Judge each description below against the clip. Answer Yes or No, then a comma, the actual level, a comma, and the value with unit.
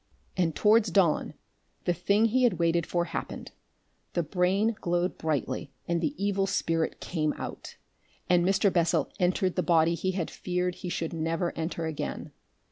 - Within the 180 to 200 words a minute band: No, average, 160 wpm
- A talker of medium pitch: Yes, medium, 175 Hz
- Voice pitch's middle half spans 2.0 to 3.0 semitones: Yes, narrow, 2.4 semitones